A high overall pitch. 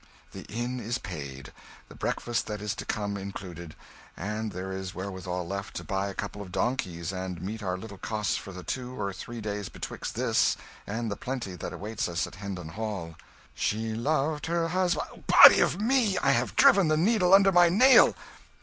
No: low, 105 Hz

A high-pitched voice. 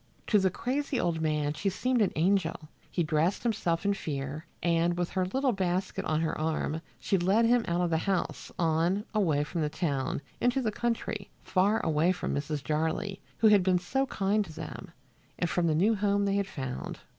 No: medium, 180 Hz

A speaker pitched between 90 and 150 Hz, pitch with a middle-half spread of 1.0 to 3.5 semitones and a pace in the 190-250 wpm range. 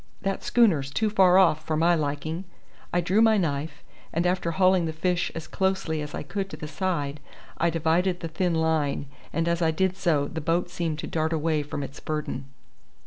No: medium, 165 Hz; average, 3.0 semitones; average, 200 wpm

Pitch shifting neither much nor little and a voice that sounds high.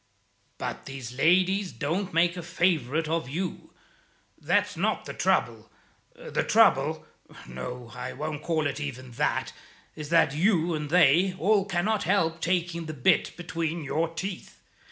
No: average, 3.5 semitones; medium, 165 Hz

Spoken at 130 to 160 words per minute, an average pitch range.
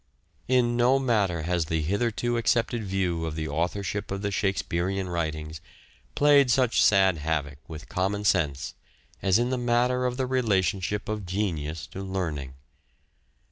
No: average, 150 wpm; wide, 6.4 semitones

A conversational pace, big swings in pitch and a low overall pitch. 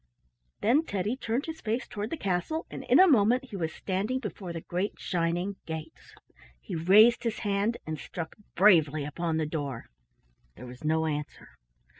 No: average, 170 wpm; wide, 5.9 semitones; high, 190 Hz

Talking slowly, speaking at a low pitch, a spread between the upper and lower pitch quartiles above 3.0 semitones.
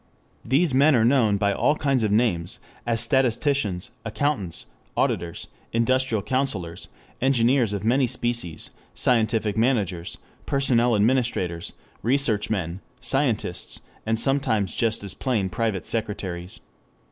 Yes: slow, 115 wpm; low, 115 Hz; average, 4.5 semitones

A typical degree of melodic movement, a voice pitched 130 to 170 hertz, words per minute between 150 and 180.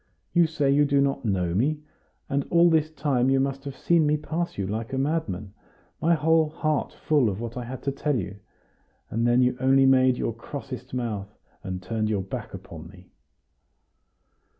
No: average, 4.7 semitones; low, 135 Hz; average, 190 wpm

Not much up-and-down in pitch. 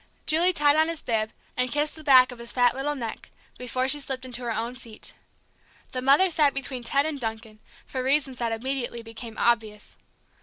No: average, 3.4 semitones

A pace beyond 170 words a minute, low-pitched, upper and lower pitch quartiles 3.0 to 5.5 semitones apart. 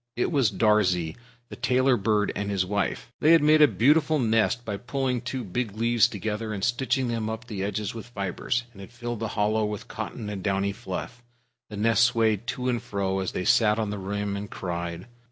Yes: fast, 205 wpm; low, 110 Hz; average, 3.3 semitones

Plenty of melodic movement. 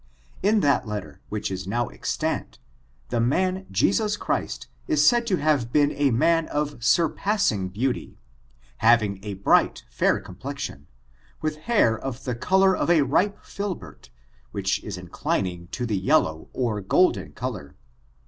Yes: wide, 8.7 semitones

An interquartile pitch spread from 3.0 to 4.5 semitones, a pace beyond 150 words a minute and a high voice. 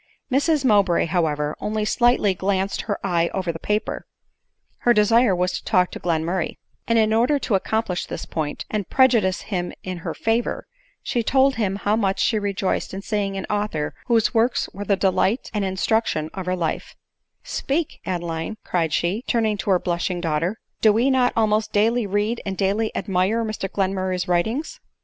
Yes: average, 3.6 semitones; average, 185 wpm; high, 200 Hz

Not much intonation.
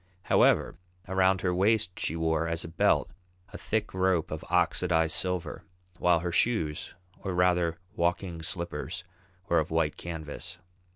Yes: narrow, 2.2 semitones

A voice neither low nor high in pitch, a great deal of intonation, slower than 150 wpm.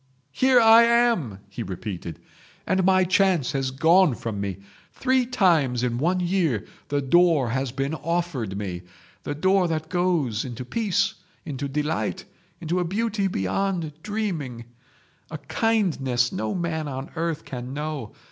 Yes: medium, 155 Hz; wide, 6.9 semitones; average, 140 wpm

